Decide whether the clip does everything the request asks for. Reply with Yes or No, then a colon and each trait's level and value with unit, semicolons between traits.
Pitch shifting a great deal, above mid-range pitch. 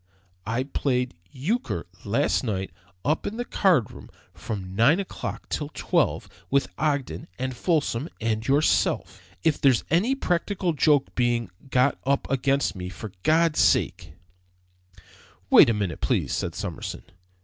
No: wide, 6.2 semitones; low, 130 Hz